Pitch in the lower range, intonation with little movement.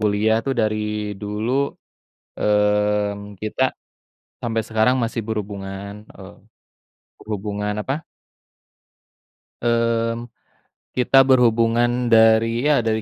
Yes: low, 110 Hz; narrow, 2.1 semitones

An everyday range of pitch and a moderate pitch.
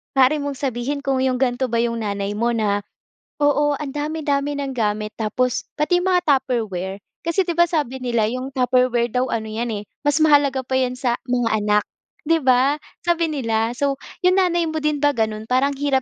No: average, 3.7 semitones; very high, 260 Hz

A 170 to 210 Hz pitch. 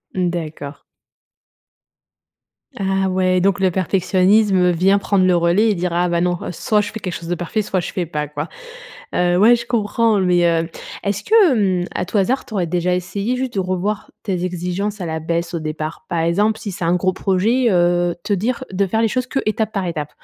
Yes: medium, 185 Hz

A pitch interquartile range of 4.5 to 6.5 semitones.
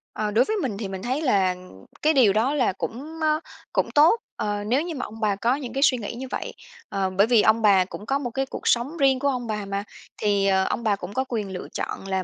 Yes: average, 5.0 semitones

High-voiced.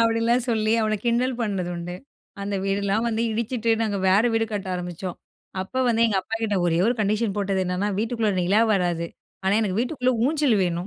Yes: high, 215 Hz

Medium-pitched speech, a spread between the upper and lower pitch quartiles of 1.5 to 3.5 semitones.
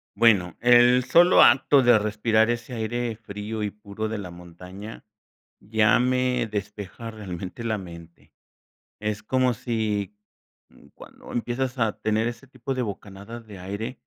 No: low, 110 Hz; average, 2.9 semitones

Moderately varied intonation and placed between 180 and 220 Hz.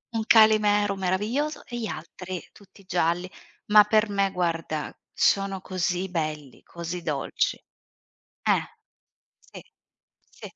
Yes: average, 3.4 semitones; high, 190 Hz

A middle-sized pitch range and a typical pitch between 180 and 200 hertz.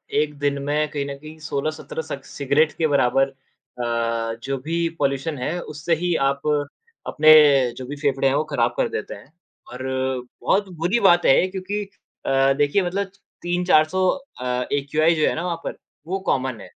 No: average, 4.1 semitones; medium, 150 Hz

